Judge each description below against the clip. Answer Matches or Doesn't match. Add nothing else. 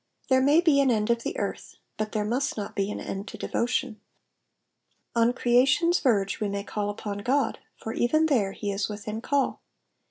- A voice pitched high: Matches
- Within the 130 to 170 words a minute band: Doesn't match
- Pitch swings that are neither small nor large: Matches